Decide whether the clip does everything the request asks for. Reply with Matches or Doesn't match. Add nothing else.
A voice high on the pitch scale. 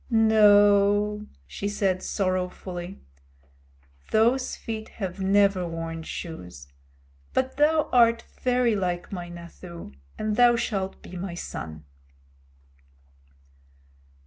Matches